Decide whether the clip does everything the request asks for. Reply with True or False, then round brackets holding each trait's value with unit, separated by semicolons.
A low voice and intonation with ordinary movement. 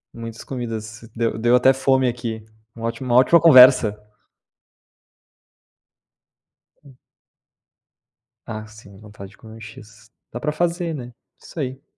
True (120 Hz; 3.0 semitones)